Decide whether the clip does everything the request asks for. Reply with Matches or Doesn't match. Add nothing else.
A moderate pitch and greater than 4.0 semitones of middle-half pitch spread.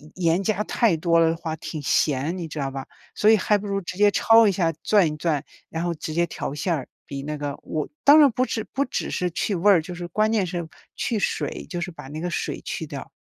Matches